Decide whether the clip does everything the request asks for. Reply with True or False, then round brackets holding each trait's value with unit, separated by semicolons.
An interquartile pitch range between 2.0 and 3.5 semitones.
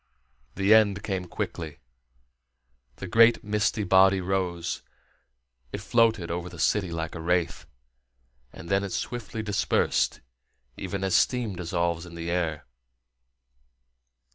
True (3.1 semitones)